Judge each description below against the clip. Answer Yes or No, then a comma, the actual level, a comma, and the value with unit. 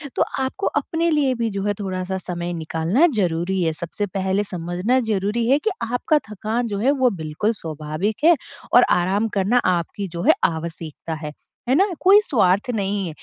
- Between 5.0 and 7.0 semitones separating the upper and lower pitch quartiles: Yes, wide, 5.6 semitones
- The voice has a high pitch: Yes, high, 195 Hz